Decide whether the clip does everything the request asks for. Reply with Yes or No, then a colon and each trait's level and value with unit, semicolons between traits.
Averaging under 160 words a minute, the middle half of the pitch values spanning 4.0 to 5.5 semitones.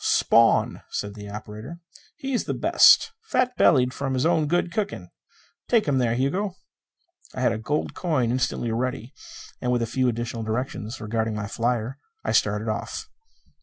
No: average, 165 wpm; average, 4.8 semitones